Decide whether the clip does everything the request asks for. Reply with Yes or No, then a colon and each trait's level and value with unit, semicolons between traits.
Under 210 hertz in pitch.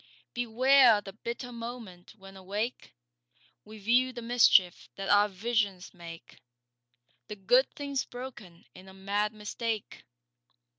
No: high, 215 Hz